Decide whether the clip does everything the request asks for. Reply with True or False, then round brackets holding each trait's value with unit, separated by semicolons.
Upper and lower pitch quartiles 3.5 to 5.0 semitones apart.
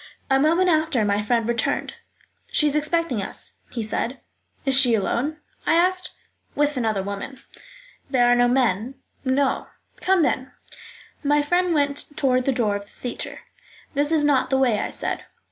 True (3.9 semitones)